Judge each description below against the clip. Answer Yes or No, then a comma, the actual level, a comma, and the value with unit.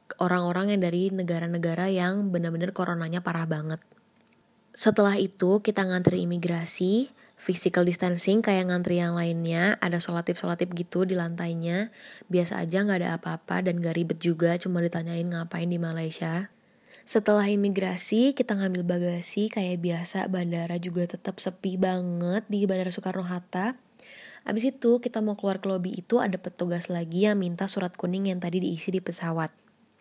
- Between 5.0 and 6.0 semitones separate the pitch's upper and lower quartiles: No, narrow, 2.4 semitones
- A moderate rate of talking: No, fast, 150 wpm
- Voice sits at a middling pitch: Yes, medium, 180 Hz